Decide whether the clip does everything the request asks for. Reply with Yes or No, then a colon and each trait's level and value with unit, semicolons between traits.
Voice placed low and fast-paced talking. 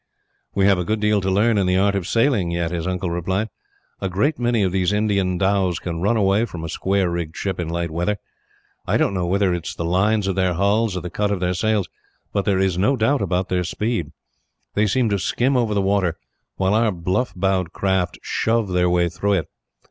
Yes: very low, 95 Hz; fast, 230 wpm